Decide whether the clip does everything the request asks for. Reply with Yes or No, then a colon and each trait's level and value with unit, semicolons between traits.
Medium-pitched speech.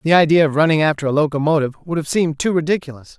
Yes: medium, 155 Hz